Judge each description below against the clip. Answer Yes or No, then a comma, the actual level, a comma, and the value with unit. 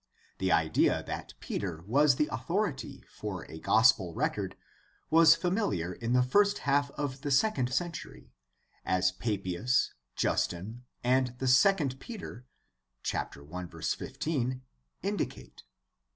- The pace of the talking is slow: Yes, slow, 110 wpm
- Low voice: Yes, low, 125 Hz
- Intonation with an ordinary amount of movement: No, wide, 8.0 semitones